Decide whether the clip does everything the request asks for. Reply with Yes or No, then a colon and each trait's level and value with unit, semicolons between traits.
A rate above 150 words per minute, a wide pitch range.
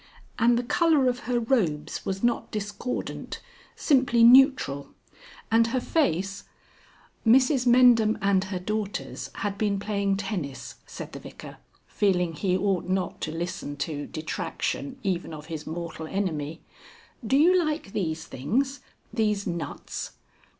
No: slow, 135 wpm; wide, 6.0 semitones